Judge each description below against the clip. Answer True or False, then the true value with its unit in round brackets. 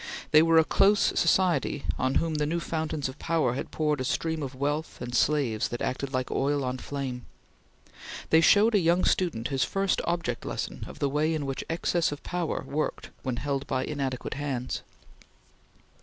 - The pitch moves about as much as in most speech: True (3.8 semitones)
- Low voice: False (145 Hz)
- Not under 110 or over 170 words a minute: False (185 wpm)